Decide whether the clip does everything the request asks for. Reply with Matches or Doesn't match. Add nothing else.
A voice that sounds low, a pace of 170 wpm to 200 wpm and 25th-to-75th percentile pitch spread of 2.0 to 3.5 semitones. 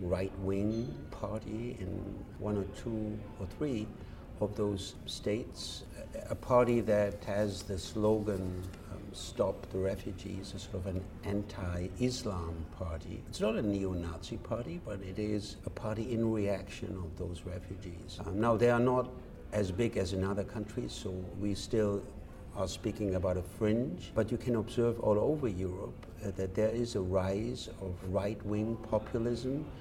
Doesn't match